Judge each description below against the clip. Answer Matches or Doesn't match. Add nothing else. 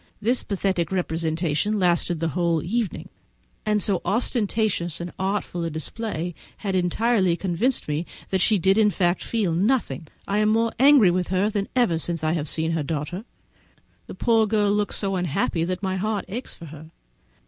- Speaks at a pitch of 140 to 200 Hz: Matches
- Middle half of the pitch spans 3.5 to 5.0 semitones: Matches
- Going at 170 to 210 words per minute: Matches